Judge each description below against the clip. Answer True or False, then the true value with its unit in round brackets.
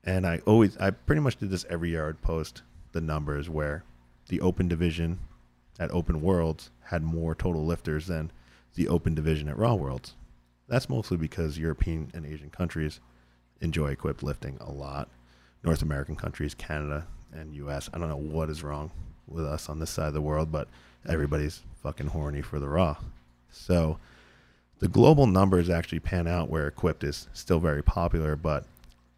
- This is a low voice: True (80 Hz)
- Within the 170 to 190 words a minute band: True (175 wpm)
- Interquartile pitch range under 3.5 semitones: True (2.9 semitones)